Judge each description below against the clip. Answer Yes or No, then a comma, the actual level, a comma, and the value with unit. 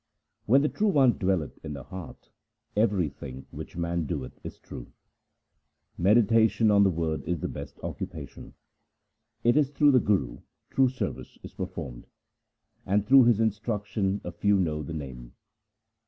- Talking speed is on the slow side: No, average, 150 wpm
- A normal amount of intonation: No, wide, 5.8 semitones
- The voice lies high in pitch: No, low, 100 Hz